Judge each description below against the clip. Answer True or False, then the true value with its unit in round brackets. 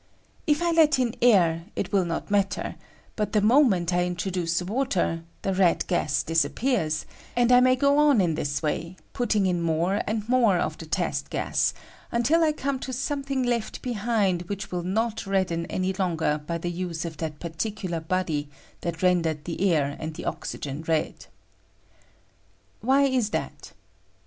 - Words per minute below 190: True (165 wpm)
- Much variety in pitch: True (6.2 semitones)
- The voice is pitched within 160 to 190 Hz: True (185 Hz)